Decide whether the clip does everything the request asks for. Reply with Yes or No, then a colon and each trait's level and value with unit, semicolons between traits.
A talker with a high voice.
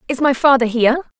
Yes: very high, 260 Hz